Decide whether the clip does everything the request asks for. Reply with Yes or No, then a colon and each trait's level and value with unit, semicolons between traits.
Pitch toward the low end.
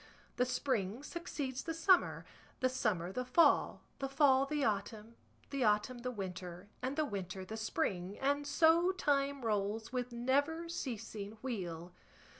No: very high, 250 Hz